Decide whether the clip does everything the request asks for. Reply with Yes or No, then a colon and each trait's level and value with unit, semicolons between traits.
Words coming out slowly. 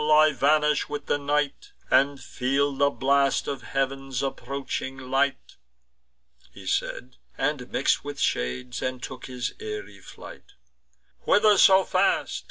Yes: slow, 130 wpm